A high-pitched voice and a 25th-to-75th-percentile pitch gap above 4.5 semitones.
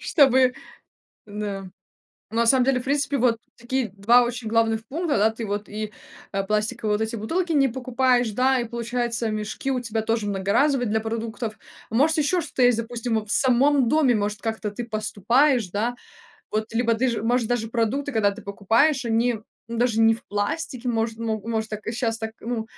No: high, 230 Hz; narrow, 2.5 semitones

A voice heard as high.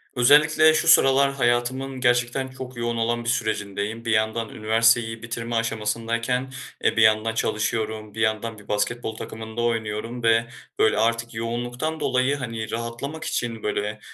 No: low, 115 Hz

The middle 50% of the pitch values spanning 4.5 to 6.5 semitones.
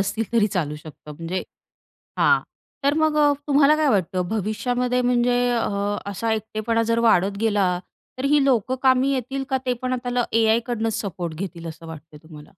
Yes: wide, 5.5 semitones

